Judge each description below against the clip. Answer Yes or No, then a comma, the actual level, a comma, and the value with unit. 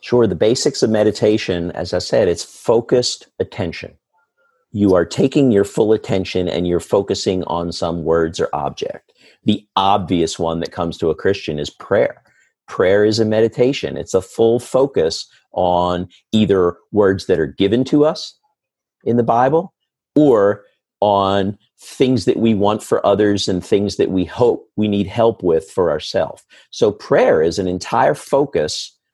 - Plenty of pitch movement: No, average, 4.8 semitones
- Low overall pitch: Yes, low, 105 Hz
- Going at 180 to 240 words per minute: No, average, 165 wpm